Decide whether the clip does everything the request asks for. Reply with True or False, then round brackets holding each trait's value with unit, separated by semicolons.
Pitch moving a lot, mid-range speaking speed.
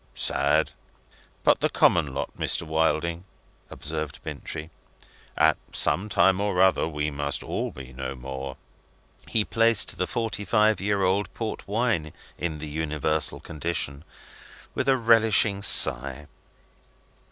False (5.7 semitones; 130 wpm)